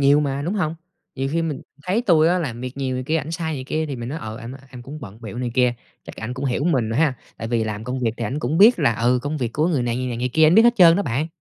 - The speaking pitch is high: No, low, 135 Hz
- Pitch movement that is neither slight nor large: Yes, average, 4.8 semitones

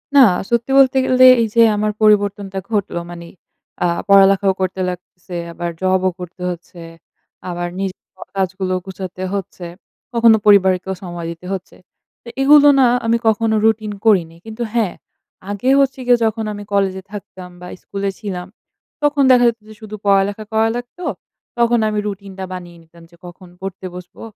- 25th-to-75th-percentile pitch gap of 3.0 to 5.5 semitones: Yes, average, 3.3 semitones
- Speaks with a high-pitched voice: Yes, high, 200 Hz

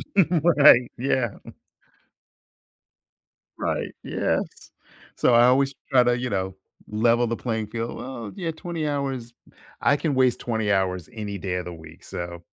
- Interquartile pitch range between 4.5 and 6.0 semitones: Yes, average, 5.0 semitones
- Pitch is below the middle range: Yes, low, 120 Hz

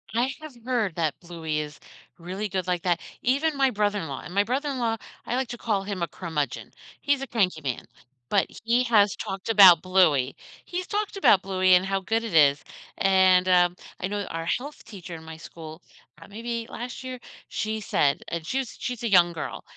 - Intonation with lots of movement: Yes, wide, 5.7 semitones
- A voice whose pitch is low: No, high, 195 Hz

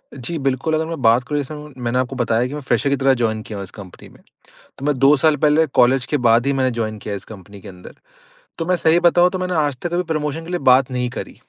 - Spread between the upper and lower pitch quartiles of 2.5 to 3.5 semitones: No, average, 4.8 semitones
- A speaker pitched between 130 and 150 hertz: Yes, low, 135 Hz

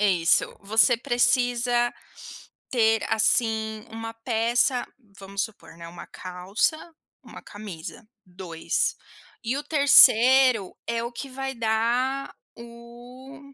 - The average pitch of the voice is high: Yes, high, 230 Hz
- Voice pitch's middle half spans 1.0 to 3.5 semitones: Yes, average, 2.7 semitones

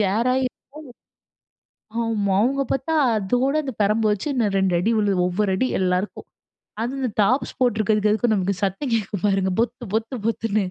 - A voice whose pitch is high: Yes, high, 215 Hz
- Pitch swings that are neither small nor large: Yes, average, 3.8 semitones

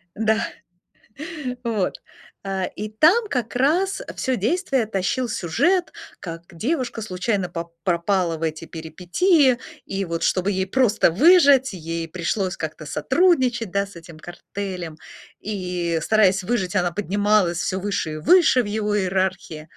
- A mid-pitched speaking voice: No, high, 195 Hz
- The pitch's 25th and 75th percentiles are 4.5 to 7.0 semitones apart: Yes, wide, 5.5 semitones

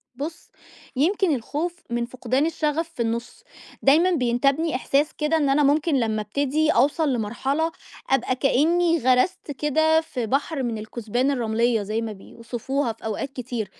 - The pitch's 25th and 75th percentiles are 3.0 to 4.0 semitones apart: No, average, 4.7 semitones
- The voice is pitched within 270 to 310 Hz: Yes, very high, 275 Hz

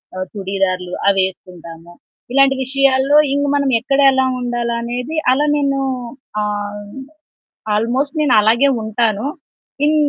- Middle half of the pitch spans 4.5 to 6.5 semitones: Yes, average, 5.1 semitones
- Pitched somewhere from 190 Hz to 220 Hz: No, high, 235 Hz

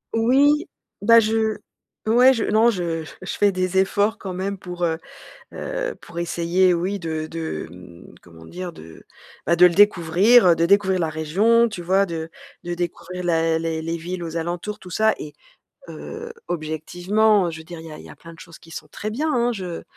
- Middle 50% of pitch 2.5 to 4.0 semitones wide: No, average, 4.4 semitones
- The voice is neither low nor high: Yes, medium, 180 Hz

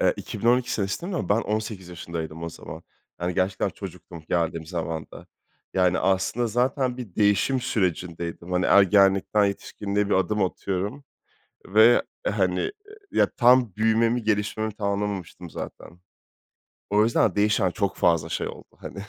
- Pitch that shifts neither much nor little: Yes, average, 3.5 semitones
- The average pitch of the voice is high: No, low, 100 Hz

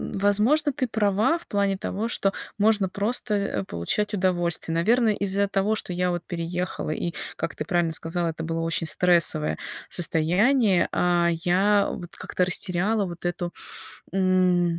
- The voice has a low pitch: No, medium, 185 Hz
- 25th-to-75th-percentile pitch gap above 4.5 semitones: No, average, 3.0 semitones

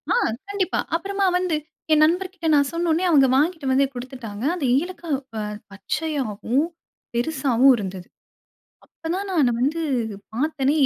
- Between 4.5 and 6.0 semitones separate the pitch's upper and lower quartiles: Yes, average, 4.9 semitones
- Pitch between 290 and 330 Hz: Yes, very high, 295 Hz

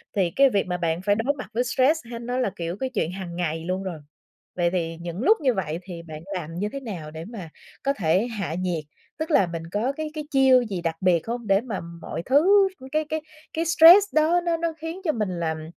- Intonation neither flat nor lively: No, wide, 8.3 semitones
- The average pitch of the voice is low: No, high, 205 Hz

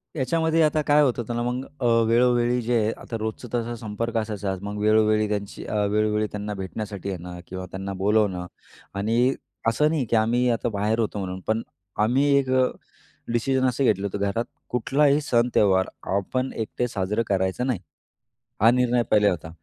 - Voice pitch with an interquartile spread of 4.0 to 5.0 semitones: No, average, 3.4 semitones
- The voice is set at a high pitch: No, low, 110 Hz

